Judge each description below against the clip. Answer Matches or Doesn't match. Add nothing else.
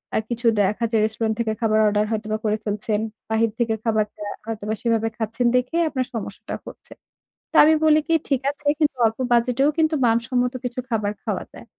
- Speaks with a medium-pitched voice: Doesn't match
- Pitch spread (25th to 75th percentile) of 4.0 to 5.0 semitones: Doesn't match